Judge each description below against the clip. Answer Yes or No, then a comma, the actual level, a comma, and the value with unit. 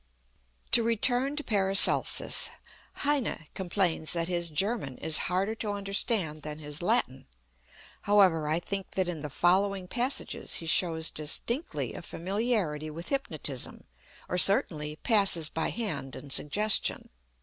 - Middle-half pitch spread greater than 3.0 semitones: Yes, average, 5.1 semitones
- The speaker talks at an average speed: No, slow, 130 wpm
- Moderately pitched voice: Yes, medium, 180 Hz